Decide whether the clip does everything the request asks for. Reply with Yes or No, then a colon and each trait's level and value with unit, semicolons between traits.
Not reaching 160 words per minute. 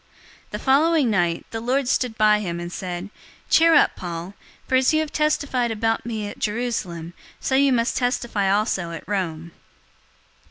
No: average, 170 wpm